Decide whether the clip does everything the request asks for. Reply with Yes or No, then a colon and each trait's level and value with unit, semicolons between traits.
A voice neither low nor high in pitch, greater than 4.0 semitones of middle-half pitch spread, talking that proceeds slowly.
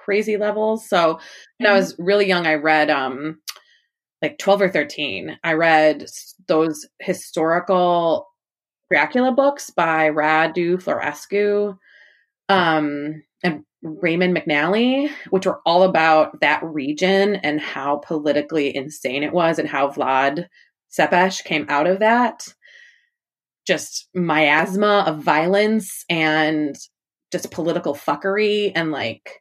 Yes: medium, 170 Hz; average, 4.7 semitones; slow, 120 wpm